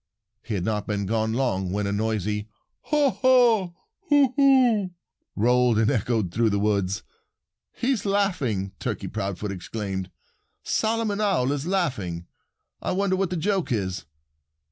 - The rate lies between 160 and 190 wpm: No, average, 140 wpm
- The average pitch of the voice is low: Yes, low, 120 Hz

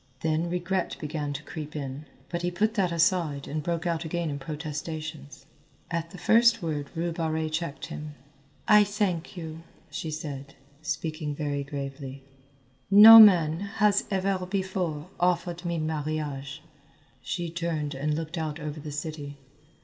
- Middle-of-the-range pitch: Yes, medium, 160 Hz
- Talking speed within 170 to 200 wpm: No, average, 150 wpm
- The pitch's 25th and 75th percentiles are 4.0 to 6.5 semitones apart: No, average, 2.8 semitones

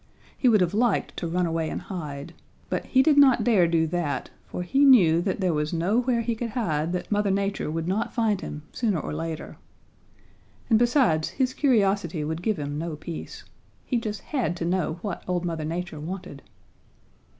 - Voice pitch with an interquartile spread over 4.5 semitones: Yes, wide, 5.5 semitones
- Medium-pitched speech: Yes, medium, 180 Hz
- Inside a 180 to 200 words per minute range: Yes, average, 190 wpm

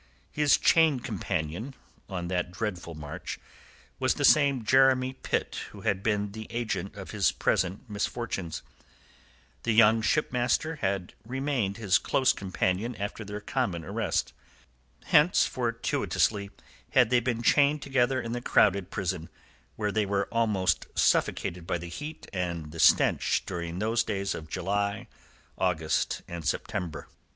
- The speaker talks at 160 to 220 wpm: No, average, 140 wpm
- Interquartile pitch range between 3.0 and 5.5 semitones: Yes, average, 4.9 semitones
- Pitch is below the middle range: Yes, low, 105 Hz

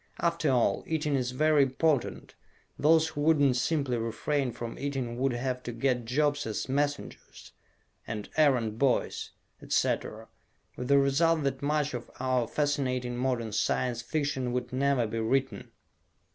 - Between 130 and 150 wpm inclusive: Yes, average, 145 wpm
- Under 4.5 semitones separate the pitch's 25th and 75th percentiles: Yes, average, 3.0 semitones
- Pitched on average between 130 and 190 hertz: Yes, low, 135 Hz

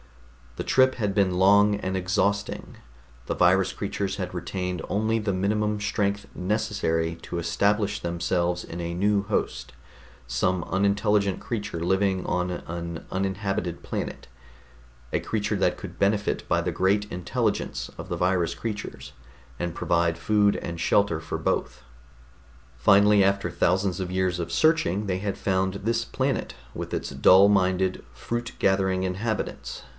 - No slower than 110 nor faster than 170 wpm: Yes, average, 140 wpm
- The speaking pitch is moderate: No, very low, 95 Hz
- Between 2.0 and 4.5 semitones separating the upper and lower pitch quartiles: Yes, narrow, 2.5 semitones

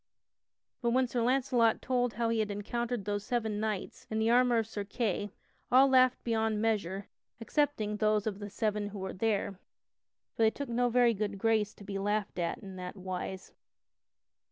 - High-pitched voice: Yes, high, 220 Hz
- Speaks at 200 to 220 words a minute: No, average, 180 wpm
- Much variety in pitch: No, narrow, 2.6 semitones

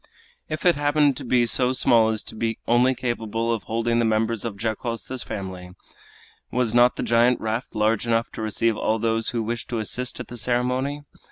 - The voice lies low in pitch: Yes, low, 115 Hz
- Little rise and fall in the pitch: Yes, narrow, 2.0 semitones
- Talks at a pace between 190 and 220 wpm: Yes, average, 195 wpm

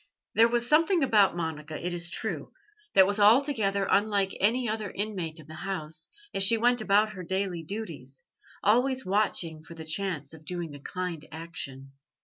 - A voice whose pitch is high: Yes, high, 195 Hz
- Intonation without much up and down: No, average, 5.0 semitones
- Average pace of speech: Yes, average, 170 wpm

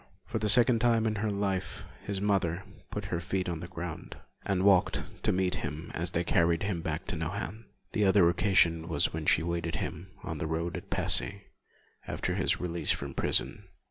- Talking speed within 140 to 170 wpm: No, average, 195 wpm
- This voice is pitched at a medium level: No, very low, 90 Hz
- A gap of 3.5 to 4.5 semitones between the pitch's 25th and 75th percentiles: No, average, 3.1 semitones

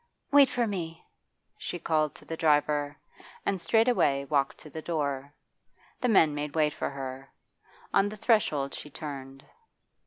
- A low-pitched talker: No, medium, 150 Hz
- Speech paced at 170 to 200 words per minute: No, average, 150 wpm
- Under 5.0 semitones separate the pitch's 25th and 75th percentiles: Yes, average, 4.6 semitones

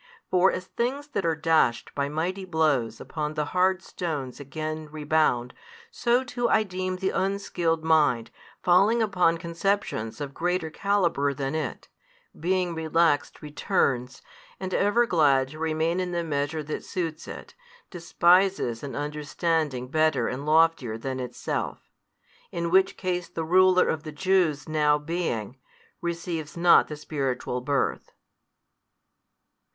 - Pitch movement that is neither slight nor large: Yes, average, 3.9 semitones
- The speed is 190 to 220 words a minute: No, slow, 135 wpm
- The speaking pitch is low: No, medium, 160 Hz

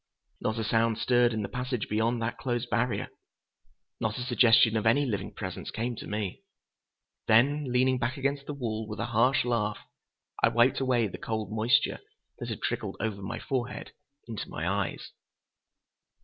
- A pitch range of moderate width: No, narrow, 2.3 semitones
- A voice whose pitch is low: Yes, low, 115 Hz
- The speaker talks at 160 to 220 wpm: Yes, average, 170 wpm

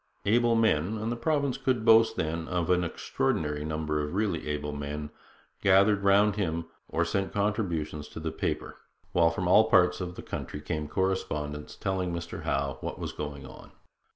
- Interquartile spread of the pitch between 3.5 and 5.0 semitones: No, wide, 5.4 semitones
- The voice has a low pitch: Yes, very low, 90 Hz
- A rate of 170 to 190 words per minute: Yes, average, 175 wpm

